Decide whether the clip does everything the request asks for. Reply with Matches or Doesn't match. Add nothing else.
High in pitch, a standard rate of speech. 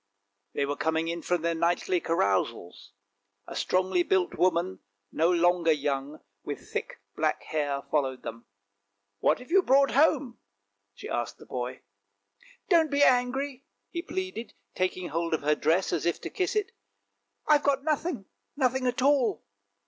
Doesn't match